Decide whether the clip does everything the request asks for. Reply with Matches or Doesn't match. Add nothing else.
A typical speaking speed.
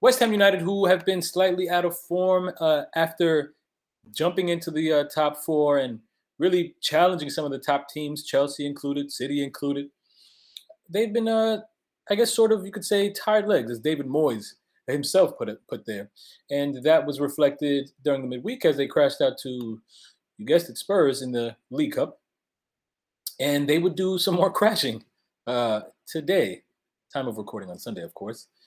Matches